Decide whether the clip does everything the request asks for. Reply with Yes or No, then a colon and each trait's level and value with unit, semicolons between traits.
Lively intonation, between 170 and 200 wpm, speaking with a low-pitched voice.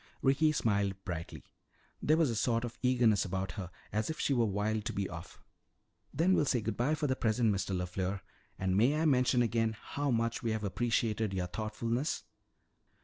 No: average, 4.1 semitones; average, 190 wpm; low, 115 Hz